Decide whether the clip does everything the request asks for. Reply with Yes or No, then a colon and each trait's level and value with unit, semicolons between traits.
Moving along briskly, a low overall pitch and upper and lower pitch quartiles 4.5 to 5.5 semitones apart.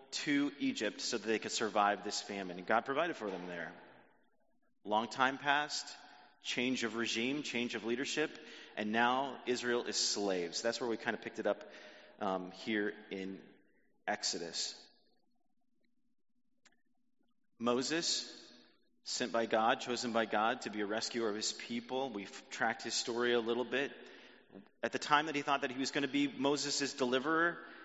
No: average, 165 wpm; low, 125 Hz; average, 4.9 semitones